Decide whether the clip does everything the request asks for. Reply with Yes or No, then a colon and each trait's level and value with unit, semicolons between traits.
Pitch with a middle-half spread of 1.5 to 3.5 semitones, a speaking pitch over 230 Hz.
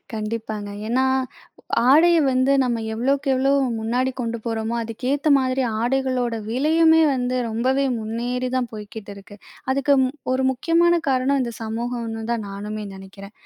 Yes: average, 3.1 semitones; high, 245 Hz